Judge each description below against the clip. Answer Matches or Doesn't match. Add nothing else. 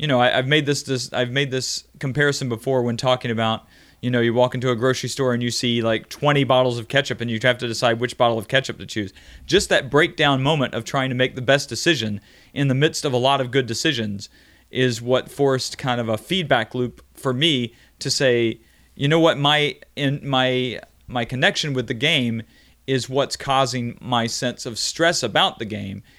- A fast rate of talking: Matches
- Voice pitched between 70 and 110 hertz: Doesn't match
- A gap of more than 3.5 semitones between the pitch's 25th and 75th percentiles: Doesn't match